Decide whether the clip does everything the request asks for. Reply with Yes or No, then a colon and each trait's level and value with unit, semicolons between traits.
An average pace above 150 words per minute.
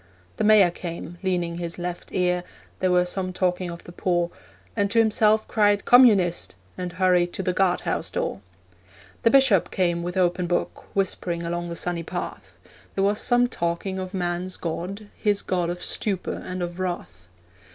Yes: average, 170 wpm